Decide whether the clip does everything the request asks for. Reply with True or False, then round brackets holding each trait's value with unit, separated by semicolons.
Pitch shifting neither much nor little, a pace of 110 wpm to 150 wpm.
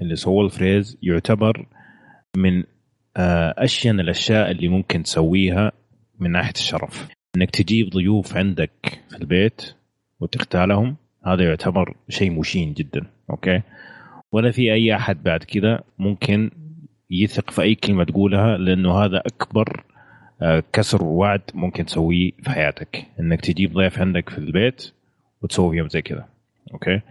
True (3.1 semitones; 125 wpm)